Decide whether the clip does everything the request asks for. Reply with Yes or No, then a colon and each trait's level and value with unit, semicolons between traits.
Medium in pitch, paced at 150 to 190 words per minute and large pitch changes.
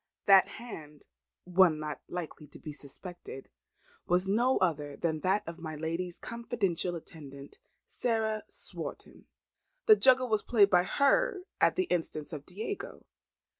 No: medium, 180 Hz; slow, 135 wpm; wide, 6.1 semitones